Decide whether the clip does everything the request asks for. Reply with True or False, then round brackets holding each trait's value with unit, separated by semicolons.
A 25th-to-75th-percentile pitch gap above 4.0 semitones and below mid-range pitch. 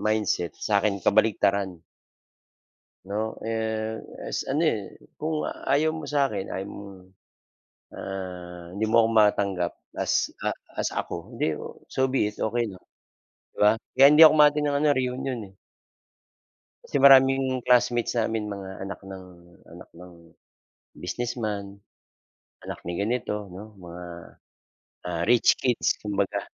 True (4.8 semitones; 110 Hz)